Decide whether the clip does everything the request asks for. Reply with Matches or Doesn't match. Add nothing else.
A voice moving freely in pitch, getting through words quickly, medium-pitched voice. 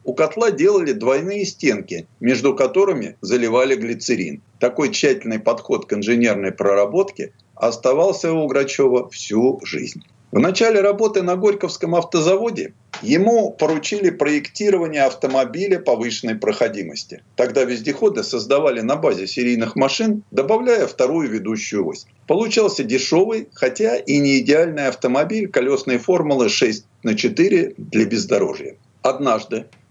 Doesn't match